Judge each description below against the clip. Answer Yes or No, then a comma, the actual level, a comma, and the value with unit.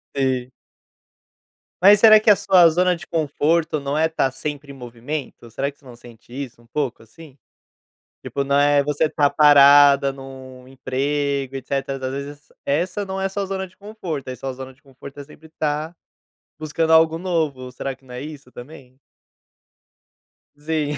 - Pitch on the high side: No, medium, 145 Hz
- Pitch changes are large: No, average, 3.3 semitones